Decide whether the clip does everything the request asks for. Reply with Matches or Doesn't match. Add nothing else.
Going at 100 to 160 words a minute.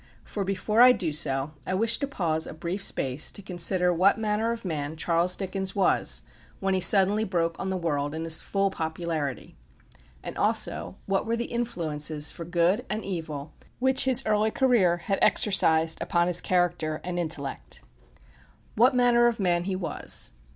Doesn't match